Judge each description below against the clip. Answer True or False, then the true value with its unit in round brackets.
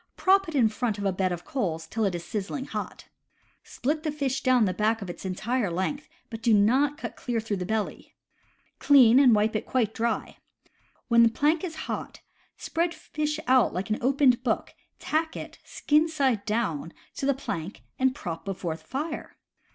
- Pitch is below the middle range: False (235 Hz)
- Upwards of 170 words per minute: True (180 wpm)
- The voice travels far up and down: True (5.7 semitones)